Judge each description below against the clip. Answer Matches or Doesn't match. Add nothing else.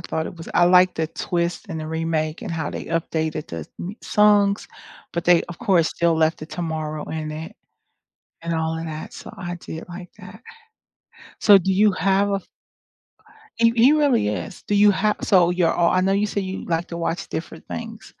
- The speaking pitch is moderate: Matches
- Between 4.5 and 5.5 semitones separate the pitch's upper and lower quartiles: Doesn't match